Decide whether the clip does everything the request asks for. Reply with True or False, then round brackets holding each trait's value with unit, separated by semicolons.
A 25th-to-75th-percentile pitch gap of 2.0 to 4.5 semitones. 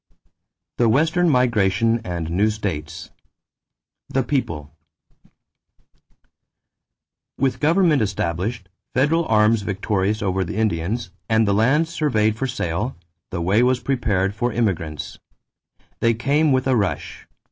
False (5.2 semitones)